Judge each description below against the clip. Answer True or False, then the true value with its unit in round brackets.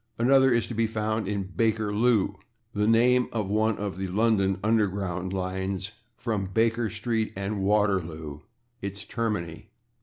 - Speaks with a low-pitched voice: True (105 Hz)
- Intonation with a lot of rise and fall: False (2.9 semitones)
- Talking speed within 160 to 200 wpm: False (140 wpm)